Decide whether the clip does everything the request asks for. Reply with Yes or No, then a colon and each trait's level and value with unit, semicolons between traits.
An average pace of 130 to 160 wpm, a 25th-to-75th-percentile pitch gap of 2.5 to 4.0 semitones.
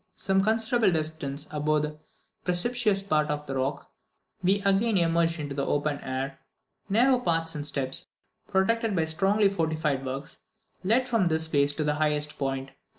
No: average, 155 wpm; average, 5.1 semitones